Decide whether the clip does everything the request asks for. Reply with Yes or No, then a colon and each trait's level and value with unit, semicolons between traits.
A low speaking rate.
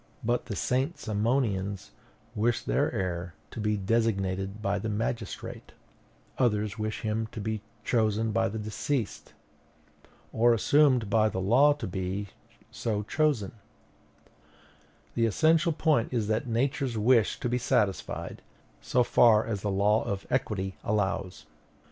Yes: slow, 130 wpm